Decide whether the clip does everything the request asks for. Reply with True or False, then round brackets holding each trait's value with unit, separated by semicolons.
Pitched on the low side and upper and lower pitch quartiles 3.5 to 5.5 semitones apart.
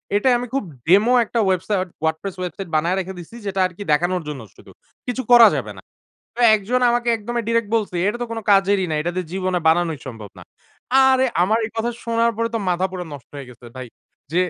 False (190 Hz; 4.7 semitones)